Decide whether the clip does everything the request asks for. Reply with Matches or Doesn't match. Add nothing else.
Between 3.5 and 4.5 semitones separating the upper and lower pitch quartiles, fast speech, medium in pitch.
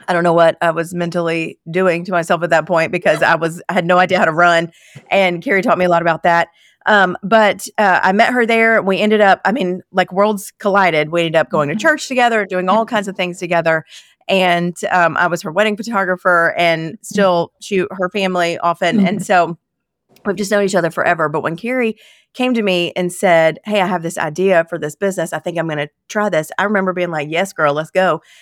Doesn't match